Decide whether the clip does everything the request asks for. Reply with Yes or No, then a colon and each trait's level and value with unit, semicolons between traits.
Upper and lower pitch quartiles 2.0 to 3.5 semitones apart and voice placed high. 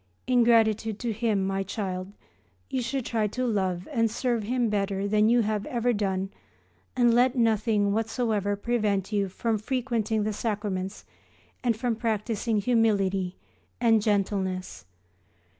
Yes: average, 2.8 semitones; high, 215 Hz